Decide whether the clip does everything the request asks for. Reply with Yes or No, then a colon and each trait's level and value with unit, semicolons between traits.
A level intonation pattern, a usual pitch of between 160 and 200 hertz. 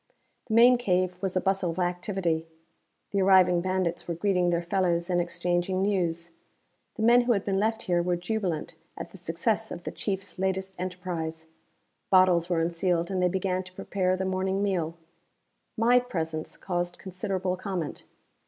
Yes: narrow, 1.9 semitones; medium, 185 Hz